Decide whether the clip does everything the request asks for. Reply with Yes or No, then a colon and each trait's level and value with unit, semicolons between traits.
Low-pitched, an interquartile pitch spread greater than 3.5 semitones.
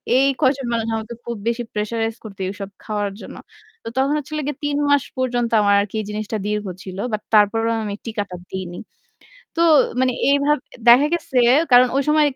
No: high, 230 Hz; average, 4.1 semitones